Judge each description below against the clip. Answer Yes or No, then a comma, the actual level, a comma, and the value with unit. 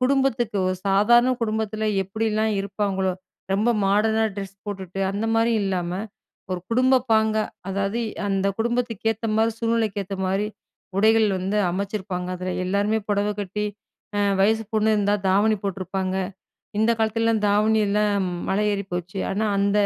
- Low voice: No, high, 210 Hz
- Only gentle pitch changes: Yes, narrow, 2.2 semitones